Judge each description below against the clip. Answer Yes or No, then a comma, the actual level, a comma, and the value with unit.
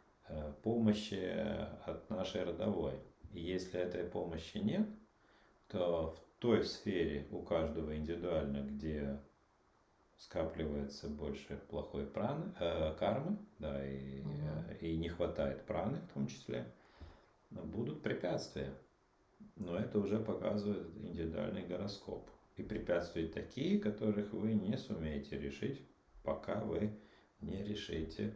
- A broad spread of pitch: Yes, wide, 6.1 semitones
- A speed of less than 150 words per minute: Yes, slow, 110 wpm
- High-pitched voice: No, very low, 85 Hz